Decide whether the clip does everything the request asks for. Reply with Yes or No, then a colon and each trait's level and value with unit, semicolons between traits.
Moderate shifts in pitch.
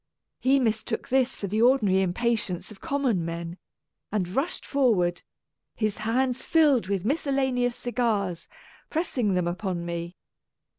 No: wide, 6.0 semitones